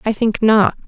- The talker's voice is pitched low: No, high, 215 Hz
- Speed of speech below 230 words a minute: Yes, fast, 205 wpm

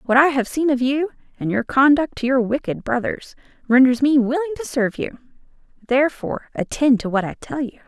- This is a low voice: No, very high, 265 Hz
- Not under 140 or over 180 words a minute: No, average, 200 wpm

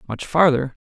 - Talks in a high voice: No, low, 135 Hz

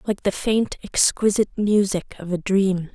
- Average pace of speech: Yes, average, 165 wpm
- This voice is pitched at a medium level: No, high, 195 Hz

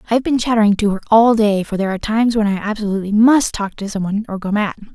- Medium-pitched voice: No, high, 210 Hz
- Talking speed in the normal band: No, fast, 265 wpm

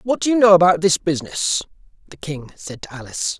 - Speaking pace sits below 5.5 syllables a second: No, 6.2 syllables/s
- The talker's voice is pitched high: No, medium, 170 Hz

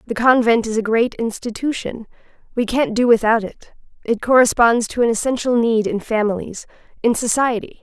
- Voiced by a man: No, female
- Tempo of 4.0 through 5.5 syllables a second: Yes, 5.2 syllables/s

